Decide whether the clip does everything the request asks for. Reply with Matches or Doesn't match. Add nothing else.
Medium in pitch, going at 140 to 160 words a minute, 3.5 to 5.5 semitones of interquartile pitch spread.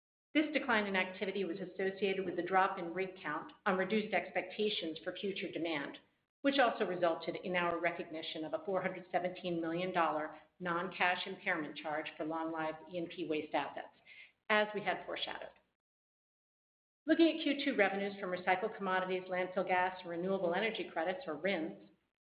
Doesn't match